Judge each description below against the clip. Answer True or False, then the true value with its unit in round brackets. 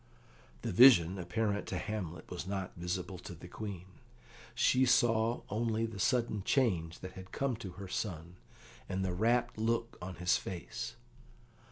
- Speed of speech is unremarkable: True (155 wpm)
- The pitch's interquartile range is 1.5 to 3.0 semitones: False (4.3 semitones)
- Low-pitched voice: True (95 Hz)